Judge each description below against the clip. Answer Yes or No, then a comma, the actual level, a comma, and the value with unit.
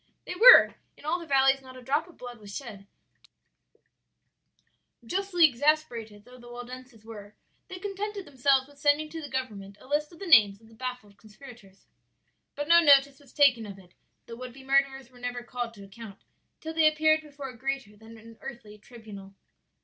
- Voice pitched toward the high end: Yes, very high, 255 Hz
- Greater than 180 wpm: Yes, average, 190 wpm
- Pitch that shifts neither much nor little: Yes, average, 4.6 semitones